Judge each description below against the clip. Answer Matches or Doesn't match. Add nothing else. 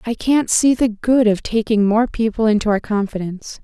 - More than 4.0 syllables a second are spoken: Matches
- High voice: Matches